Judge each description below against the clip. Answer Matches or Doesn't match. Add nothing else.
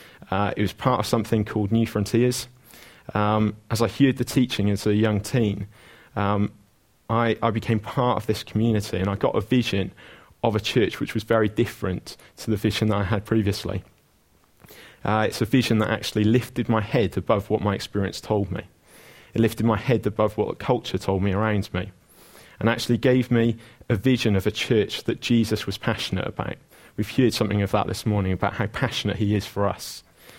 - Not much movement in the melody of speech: Matches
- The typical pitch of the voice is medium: Doesn't match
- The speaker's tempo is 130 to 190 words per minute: Doesn't match